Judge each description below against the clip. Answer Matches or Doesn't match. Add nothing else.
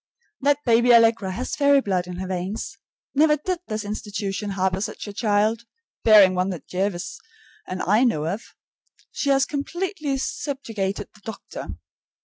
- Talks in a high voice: Matches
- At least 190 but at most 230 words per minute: Doesn't match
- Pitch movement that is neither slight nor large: Doesn't match